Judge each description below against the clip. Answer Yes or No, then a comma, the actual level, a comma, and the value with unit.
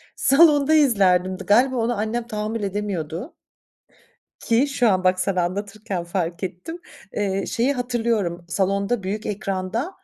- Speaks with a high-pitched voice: Yes, high, 205 Hz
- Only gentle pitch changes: No, average, 4.4 semitones